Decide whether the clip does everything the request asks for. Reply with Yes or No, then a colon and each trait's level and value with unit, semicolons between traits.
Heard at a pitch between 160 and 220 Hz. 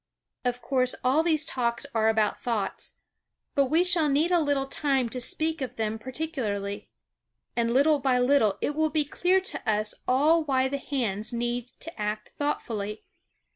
No: very high, 260 Hz